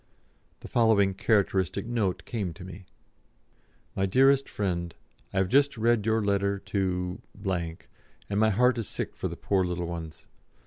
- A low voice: Yes, low, 100 Hz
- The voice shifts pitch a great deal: No, average, 3.5 semitones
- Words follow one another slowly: No, average, 150 wpm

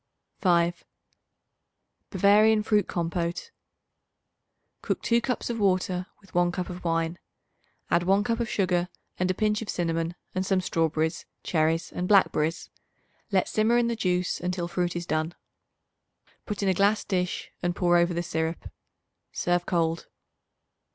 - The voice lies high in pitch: No, medium, 180 Hz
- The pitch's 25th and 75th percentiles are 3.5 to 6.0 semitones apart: No, average, 2.7 semitones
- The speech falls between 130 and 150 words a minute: Yes, average, 145 wpm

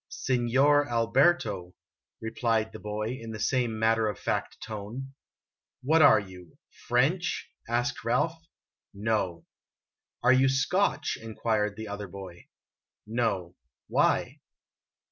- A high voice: No, low, 115 Hz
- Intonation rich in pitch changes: No, average, 3.9 semitones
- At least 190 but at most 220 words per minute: No, slow, 135 wpm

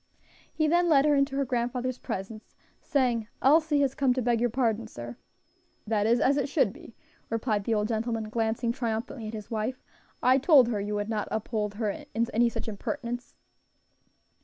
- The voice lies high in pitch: Yes, high, 235 Hz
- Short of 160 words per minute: No, average, 185 wpm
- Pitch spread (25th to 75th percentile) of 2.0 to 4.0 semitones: Yes, average, 3.3 semitones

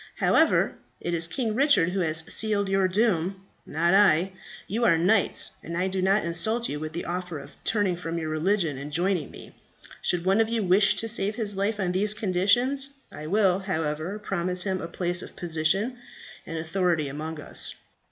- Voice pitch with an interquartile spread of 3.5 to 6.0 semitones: Yes, average, 3.8 semitones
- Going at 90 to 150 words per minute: No, average, 190 wpm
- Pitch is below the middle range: No, medium, 185 Hz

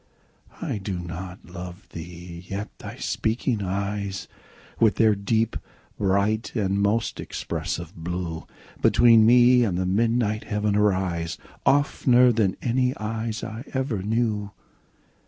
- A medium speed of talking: No, slow, 120 wpm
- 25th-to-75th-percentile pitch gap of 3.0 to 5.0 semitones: Yes, average, 3.6 semitones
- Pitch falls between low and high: No, low, 105 Hz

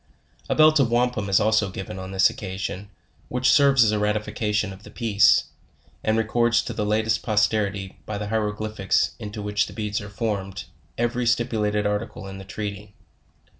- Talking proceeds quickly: No, average, 175 wpm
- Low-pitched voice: Yes, low, 105 Hz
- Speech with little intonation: Yes, narrow, 1.8 semitones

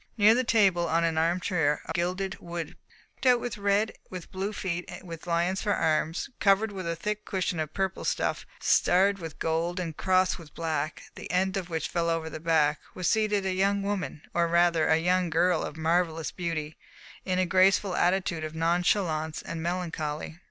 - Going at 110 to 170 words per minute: No, average, 190 wpm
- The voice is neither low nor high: Yes, medium, 175 Hz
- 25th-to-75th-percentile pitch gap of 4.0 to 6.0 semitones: No, average, 2.7 semitones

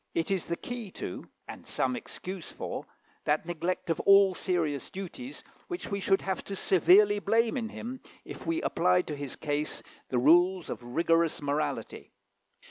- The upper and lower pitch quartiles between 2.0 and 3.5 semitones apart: No, average, 4.2 semitones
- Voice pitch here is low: No, medium, 180 Hz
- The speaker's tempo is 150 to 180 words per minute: Yes, average, 165 wpm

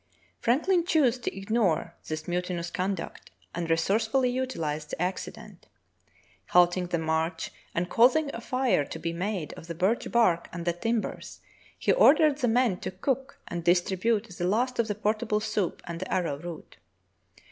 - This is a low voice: No, high, 190 Hz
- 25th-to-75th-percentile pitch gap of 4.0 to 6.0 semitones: Yes, wide, 5.6 semitones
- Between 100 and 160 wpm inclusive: No, average, 170 wpm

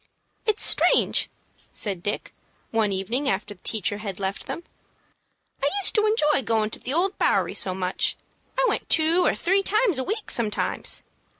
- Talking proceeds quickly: No, average, 170 wpm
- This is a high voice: Yes, high, 240 Hz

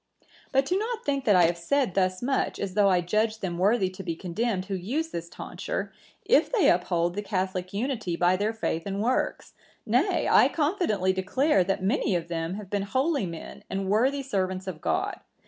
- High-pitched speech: Yes, high, 200 Hz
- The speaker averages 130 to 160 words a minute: No, average, 200 wpm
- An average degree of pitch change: No, wide, 5.9 semitones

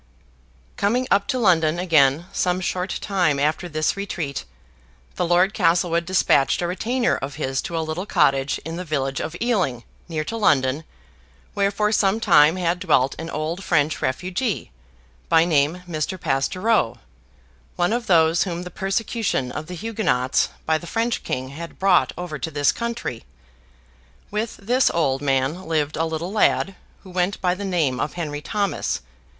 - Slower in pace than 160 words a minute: No, average, 165 wpm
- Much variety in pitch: No, average, 4.4 semitones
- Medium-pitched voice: Yes, medium, 170 Hz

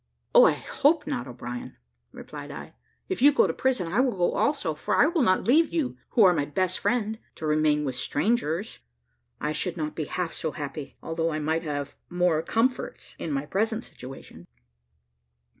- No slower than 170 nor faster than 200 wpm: Yes, average, 180 wpm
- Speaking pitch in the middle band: Yes, medium, 175 Hz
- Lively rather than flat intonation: Yes, wide, 8.2 semitones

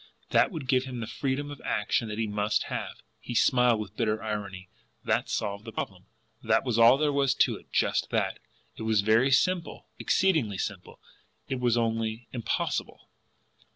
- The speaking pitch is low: Yes, low, 115 Hz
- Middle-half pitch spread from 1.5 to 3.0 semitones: No, average, 3.6 semitones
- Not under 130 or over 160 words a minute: No, average, 175 wpm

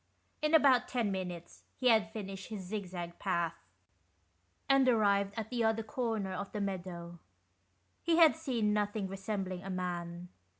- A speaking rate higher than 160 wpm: No, average, 155 wpm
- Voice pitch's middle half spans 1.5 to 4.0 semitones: Yes, average, 3.5 semitones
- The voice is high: Yes, high, 200 Hz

